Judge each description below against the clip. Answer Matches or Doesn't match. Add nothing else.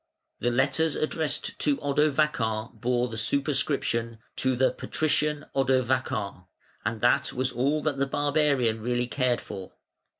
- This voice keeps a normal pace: Doesn't match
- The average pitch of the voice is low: Matches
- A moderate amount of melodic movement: Matches